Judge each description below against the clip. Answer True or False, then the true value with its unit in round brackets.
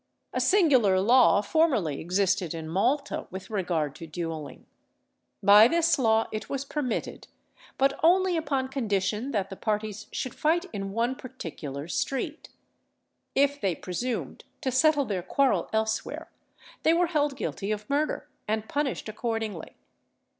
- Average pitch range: False (6.4 semitones)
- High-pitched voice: True (225 Hz)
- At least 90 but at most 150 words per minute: True (140 wpm)